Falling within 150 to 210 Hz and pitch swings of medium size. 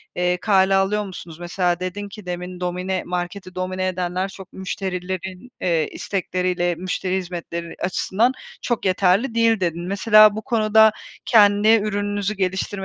No: high, 190 Hz; narrow, 2.2 semitones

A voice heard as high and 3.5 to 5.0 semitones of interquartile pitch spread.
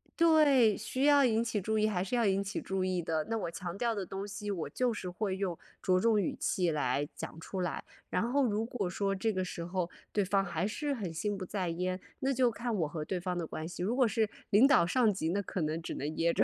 Yes: high, 195 Hz; average, 4.1 semitones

